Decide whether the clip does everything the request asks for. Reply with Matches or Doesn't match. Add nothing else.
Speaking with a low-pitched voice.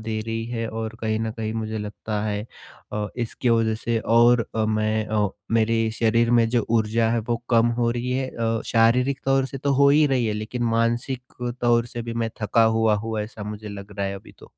Matches